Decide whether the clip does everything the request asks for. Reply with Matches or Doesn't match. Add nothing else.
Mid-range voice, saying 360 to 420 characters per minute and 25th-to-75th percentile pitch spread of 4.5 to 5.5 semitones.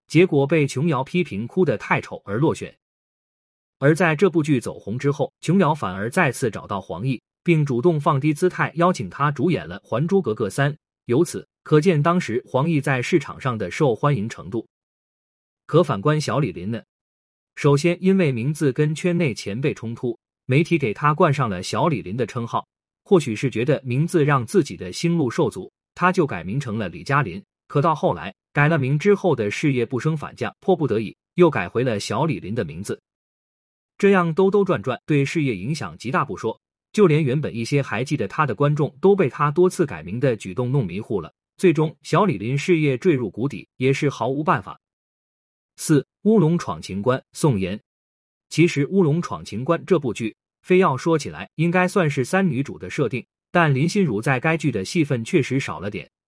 Doesn't match